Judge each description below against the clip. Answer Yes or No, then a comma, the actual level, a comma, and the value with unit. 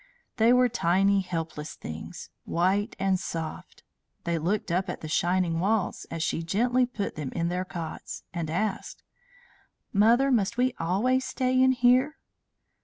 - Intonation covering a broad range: Yes, wide, 6.3 semitones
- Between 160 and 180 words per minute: No, average, 150 wpm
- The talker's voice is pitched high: Yes, high, 195 Hz